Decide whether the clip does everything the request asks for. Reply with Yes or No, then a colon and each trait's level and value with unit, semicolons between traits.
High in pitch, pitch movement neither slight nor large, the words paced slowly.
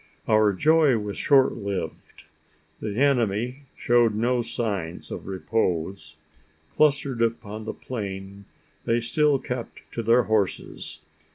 No: low, 115 Hz; average, 3.9 semitones; slow, 115 wpm